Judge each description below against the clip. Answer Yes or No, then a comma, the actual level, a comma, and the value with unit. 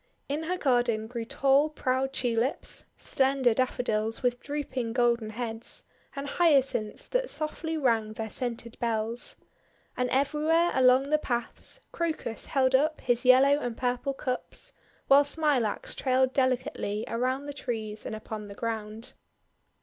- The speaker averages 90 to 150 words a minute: Yes, average, 140 wpm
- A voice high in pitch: Yes, very high, 255 Hz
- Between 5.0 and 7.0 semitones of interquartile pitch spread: No, average, 3.4 semitones